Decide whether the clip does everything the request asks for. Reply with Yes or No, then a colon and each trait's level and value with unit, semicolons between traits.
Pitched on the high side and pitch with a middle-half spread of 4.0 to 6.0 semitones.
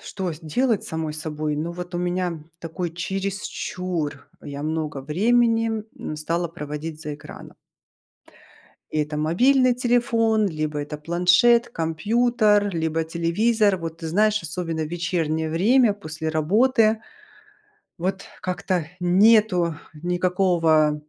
No: medium, 175 Hz; average, 4.8 semitones